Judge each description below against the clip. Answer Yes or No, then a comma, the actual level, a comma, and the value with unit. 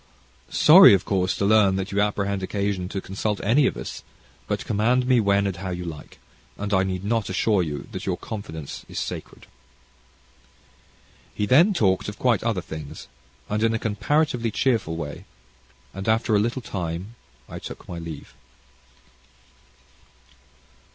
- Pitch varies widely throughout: No, average, 3.3 semitones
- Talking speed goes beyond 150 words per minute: Yes, average, 160 wpm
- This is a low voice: Yes, low, 100 Hz